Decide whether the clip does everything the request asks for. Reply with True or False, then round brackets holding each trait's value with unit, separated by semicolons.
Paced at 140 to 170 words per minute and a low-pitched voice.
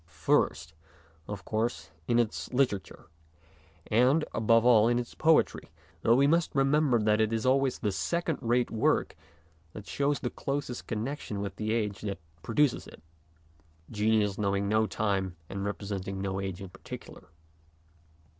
True (155 wpm; 110 Hz)